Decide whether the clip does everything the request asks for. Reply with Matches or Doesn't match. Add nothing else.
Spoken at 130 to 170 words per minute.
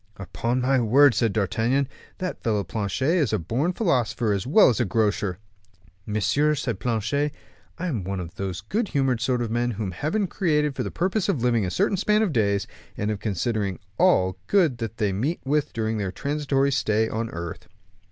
Doesn't match